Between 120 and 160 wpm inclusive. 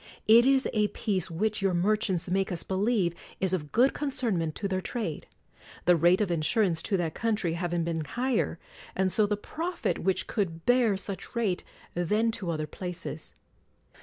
No: average, 175 wpm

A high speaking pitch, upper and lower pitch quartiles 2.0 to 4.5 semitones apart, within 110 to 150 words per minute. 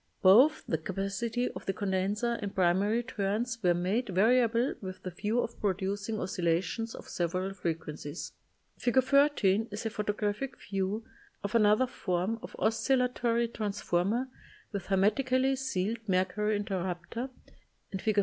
Yes: high, 205 Hz; average, 3.8 semitones; slow, 135 wpm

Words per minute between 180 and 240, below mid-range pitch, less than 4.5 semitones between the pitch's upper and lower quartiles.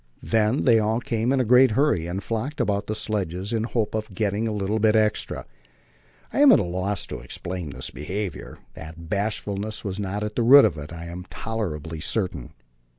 Yes: fast, 205 wpm; low, 105 Hz; average, 3.7 semitones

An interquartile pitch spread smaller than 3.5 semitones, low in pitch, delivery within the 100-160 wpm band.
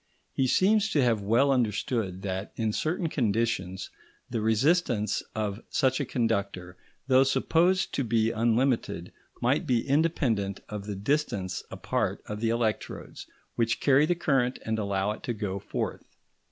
No: average, 4.6 semitones; low, 115 Hz; average, 150 wpm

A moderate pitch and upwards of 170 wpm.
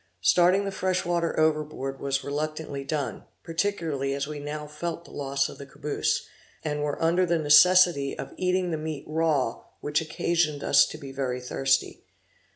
No: medium, 150 Hz; average, 165 wpm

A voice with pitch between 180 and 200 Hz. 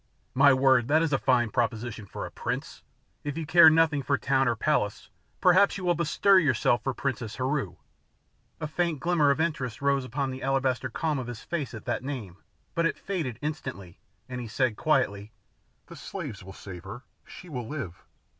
No: low, 135 Hz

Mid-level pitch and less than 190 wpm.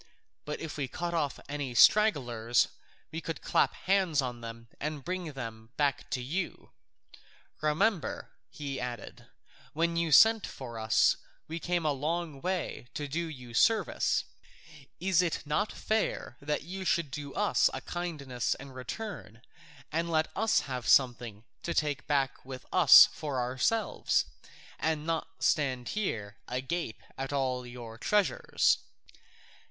Yes: medium, 145 Hz; average, 140 wpm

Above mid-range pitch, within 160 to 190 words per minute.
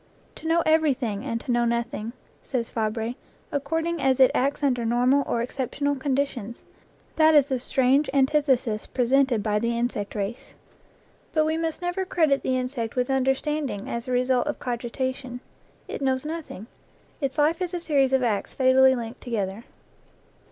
Yes: very high, 260 Hz; average, 165 wpm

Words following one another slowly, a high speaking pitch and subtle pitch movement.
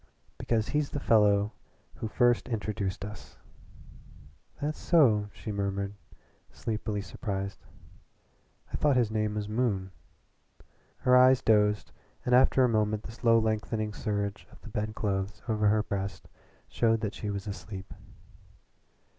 No: slow, 130 wpm; low, 105 Hz; narrow, 2.1 semitones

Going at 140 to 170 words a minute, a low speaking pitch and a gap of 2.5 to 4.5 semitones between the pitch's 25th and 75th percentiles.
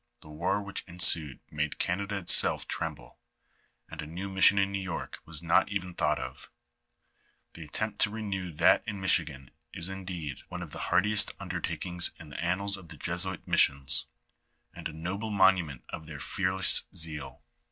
Yes: average, 165 wpm; very low, 90 Hz; average, 3.5 semitones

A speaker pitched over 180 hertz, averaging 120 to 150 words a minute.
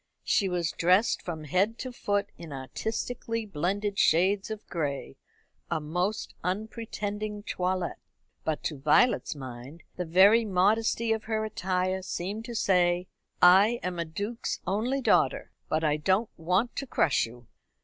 Yes: high, 190 Hz; average, 145 wpm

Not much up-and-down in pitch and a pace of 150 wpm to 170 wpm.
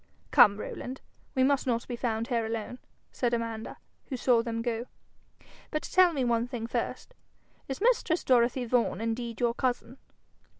Yes: narrow, 2.2 semitones; average, 160 wpm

